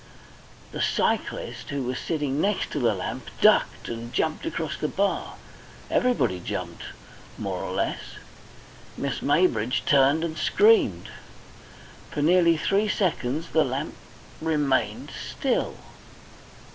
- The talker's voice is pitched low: No, medium, 150 Hz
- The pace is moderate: No, slow, 115 wpm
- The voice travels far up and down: No, average, 4.2 semitones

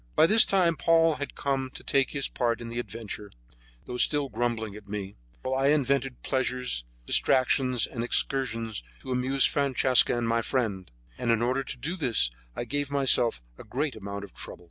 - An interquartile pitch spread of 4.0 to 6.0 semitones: No, average, 3.2 semitones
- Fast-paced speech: No, average, 185 wpm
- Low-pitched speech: Yes, low, 125 Hz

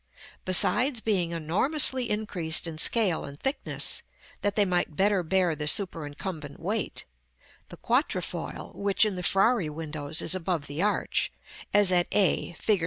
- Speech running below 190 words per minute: Yes, average, 145 wpm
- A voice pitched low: No, medium, 185 Hz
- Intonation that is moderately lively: Yes, average, 4.4 semitones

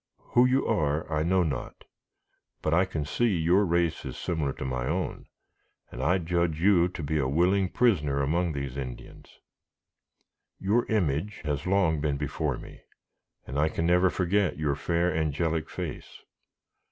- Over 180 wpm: No, average, 155 wpm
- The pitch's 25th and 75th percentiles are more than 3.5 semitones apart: Yes, average, 3.9 semitones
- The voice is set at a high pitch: No, very low, 80 Hz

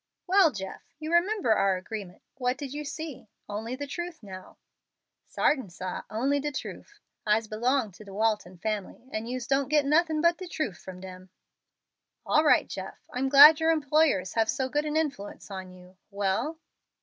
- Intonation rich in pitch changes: Yes, wide, 7.1 semitones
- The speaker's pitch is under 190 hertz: No, very high, 255 Hz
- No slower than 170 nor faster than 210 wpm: Yes, average, 175 wpm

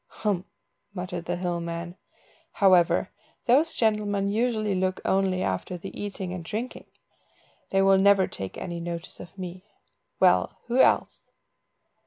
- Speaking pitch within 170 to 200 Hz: Yes, high, 190 Hz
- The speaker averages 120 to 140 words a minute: Yes, slow, 135 wpm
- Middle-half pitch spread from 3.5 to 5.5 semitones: No, average, 2.8 semitones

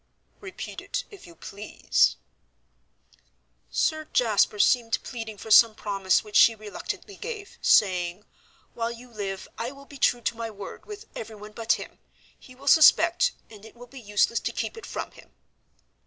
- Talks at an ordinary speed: Yes, average, 165 wpm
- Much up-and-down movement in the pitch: No, average, 4.6 semitones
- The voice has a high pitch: Yes, high, 230 Hz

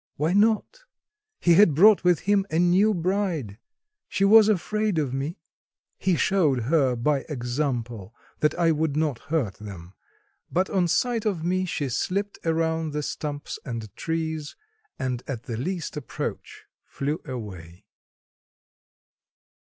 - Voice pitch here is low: No, medium, 160 Hz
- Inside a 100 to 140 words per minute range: Yes, slow, 135 wpm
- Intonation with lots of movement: Yes, wide, 6.3 semitones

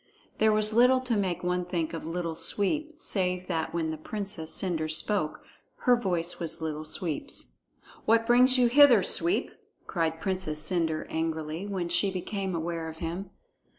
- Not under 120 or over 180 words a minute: Yes, average, 160 wpm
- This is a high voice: No, medium, 180 Hz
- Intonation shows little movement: No, average, 4.5 semitones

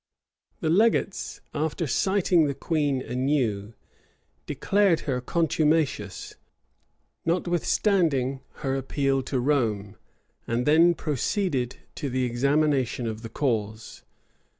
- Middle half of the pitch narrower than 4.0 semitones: No, average, 4.7 semitones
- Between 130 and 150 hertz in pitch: Yes, medium, 140 Hz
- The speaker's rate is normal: No, slow, 100 wpm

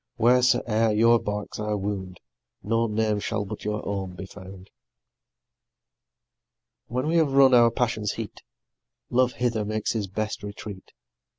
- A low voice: Yes, low, 110 Hz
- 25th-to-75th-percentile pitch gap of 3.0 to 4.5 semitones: No, narrow, 2.5 semitones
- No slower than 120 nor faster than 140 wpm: Yes, slow, 135 wpm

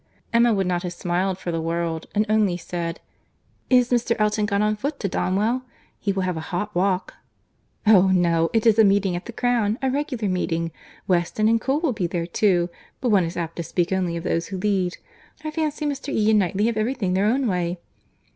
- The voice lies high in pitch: Yes, high, 200 Hz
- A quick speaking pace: Yes, fast, 210 wpm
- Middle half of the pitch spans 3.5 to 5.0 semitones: Yes, average, 4.4 semitones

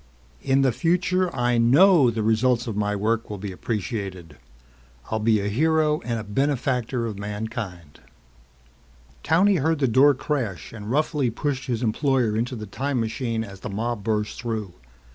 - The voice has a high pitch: No, low, 115 Hz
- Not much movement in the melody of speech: No, average, 4.3 semitones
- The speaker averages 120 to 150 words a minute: No, average, 160 wpm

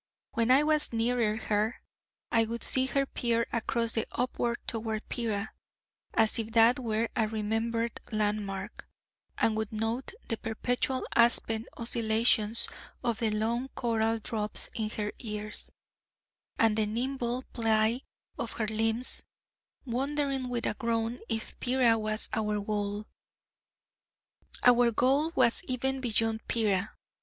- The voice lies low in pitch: No, high, 225 Hz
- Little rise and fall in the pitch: Yes, narrow, 1.9 semitones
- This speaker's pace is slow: Yes, slow, 130 wpm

